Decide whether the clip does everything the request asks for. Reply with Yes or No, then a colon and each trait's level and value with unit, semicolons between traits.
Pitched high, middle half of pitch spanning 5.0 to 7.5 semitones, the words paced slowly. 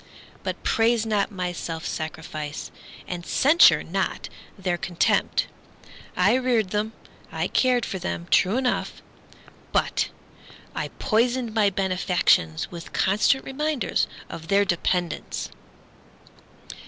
Yes: high, 195 Hz; average, 5.3 semitones; slow, 110 wpm